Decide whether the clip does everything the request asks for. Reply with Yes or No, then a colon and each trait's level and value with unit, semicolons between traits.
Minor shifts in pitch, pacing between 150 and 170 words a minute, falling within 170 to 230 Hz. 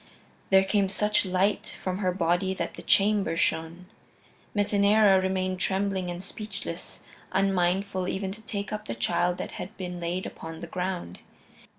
Yes: narrow, 2.0 semitones; average, 155 wpm; high, 190 Hz